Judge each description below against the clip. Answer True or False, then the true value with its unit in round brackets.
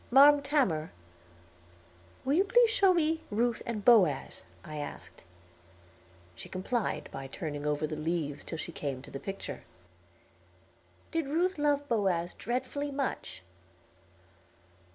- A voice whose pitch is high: True (225 Hz)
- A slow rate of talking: True (125 wpm)